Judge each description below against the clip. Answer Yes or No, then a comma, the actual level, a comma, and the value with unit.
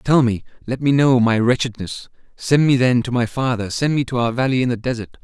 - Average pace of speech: No, fast, 230 wpm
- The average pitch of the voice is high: No, low, 125 Hz